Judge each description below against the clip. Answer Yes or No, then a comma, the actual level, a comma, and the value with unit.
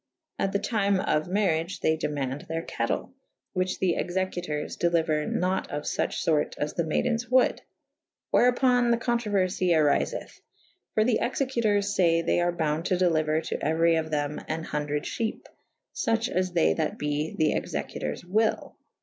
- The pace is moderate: Yes, average, 165 wpm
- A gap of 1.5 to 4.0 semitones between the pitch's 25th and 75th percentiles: No, average, 4.8 semitones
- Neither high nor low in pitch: Yes, medium, 175 Hz